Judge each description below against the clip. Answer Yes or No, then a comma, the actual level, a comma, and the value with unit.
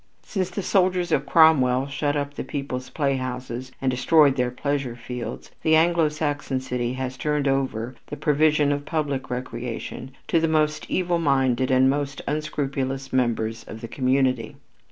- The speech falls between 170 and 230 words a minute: No, average, 160 wpm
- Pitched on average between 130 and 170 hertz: Yes, low, 135 Hz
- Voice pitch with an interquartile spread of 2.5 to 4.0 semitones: Yes, average, 3.0 semitones